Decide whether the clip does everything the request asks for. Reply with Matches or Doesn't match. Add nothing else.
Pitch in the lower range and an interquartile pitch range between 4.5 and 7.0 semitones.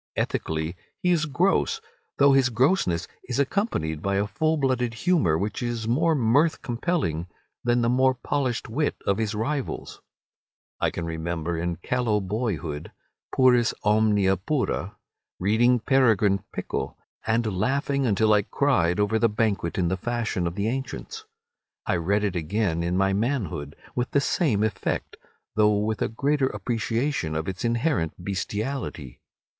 Matches